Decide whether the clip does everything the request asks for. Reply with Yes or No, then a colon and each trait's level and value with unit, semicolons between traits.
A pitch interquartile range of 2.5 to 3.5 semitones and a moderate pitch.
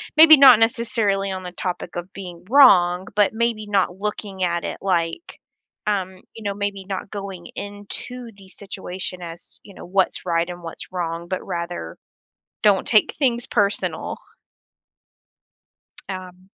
No: average, 2.8 semitones; high, 195 Hz